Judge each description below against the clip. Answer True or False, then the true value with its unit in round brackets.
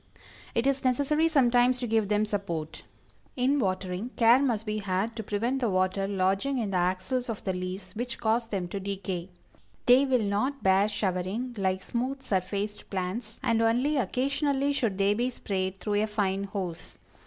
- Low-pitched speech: False (210 Hz)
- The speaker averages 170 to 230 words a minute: True (175 wpm)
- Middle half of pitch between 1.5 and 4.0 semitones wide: False (4.5 semitones)